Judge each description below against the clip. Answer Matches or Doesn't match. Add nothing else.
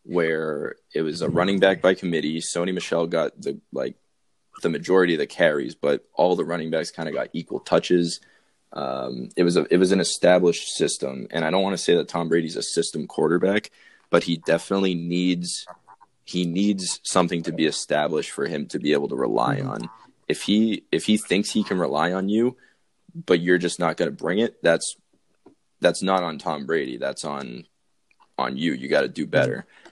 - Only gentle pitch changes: Matches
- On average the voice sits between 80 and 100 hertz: Matches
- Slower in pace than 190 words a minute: Doesn't match